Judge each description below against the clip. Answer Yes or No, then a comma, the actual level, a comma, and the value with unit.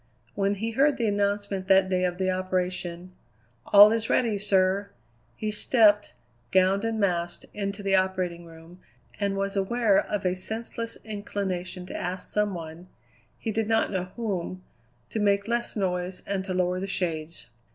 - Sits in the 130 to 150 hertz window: No, high, 195 Hz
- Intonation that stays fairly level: Yes, narrow, 2.2 semitones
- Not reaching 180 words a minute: Yes, average, 160 wpm